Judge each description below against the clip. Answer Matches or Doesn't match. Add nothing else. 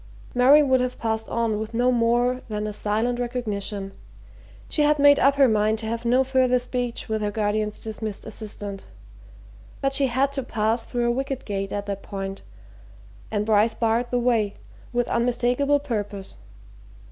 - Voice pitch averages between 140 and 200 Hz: Doesn't match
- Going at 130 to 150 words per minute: Doesn't match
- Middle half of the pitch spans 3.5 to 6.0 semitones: Doesn't match